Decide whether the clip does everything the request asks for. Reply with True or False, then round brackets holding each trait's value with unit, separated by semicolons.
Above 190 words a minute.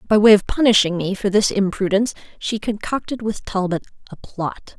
False (175 wpm)